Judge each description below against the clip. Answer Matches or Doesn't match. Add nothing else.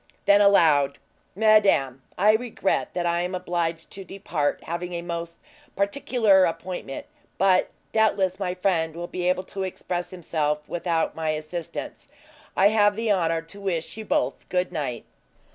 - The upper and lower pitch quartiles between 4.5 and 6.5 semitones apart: Doesn't match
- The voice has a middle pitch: Matches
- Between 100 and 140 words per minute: Doesn't match